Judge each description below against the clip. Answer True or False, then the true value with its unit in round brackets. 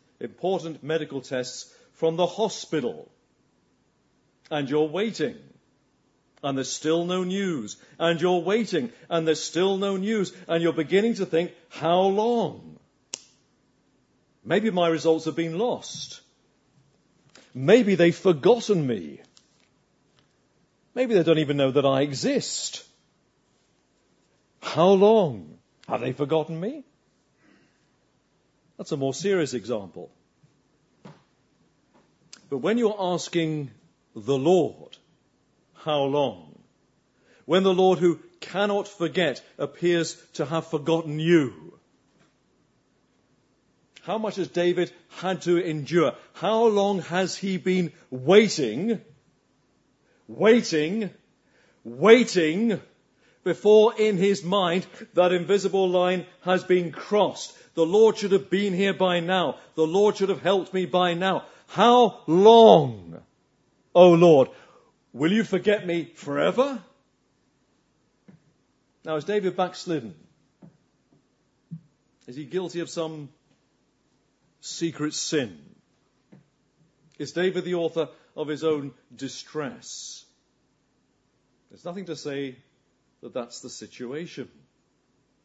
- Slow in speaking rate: True (110 wpm)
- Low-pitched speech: False (175 Hz)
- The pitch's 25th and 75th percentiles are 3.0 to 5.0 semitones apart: True (3.8 semitones)